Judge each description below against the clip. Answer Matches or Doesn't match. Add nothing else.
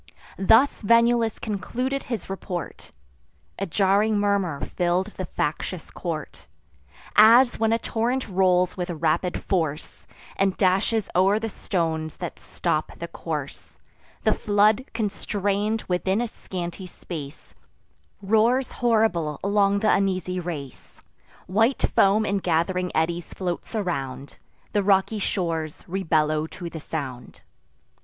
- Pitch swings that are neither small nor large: Matches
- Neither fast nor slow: Doesn't match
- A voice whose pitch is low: Doesn't match